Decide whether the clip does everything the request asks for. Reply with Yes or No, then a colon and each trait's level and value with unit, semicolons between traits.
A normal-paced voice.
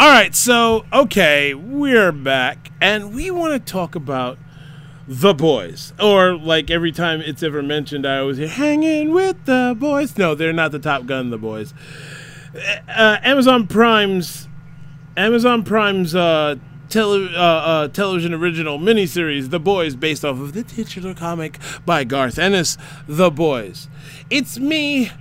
Yes: average, 150 wpm